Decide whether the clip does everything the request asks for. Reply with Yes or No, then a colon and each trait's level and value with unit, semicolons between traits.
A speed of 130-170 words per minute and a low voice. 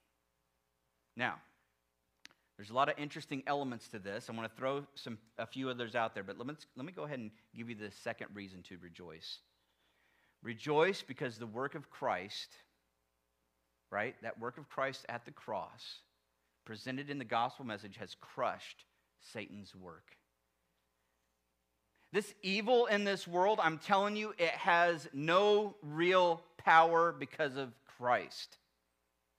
Yes: average, 150 wpm; low, 115 Hz